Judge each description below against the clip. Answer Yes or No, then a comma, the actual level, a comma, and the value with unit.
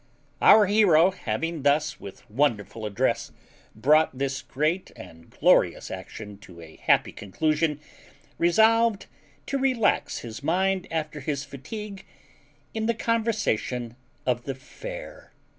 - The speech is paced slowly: Yes, slow, 120 wpm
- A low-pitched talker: No, medium, 155 Hz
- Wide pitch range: Yes, wide, 8.5 semitones